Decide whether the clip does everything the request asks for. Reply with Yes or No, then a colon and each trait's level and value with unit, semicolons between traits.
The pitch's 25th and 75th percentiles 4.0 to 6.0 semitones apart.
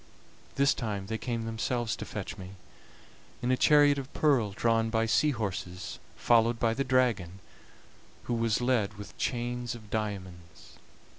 No: average, 2.9 semitones